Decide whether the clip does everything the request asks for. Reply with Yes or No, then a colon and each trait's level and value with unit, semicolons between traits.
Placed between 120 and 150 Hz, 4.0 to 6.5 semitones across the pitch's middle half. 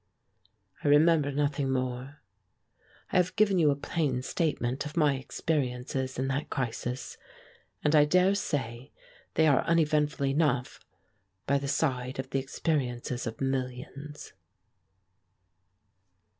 No: medium, 140 Hz; average, 2.8 semitones